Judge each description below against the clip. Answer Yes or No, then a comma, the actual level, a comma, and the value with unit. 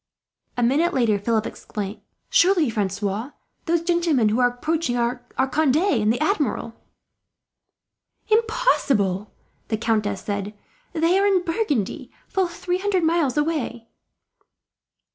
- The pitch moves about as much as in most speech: No, wide, 7.7 semitones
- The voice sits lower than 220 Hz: No, very high, 265 Hz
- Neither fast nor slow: No, slow, 120 wpm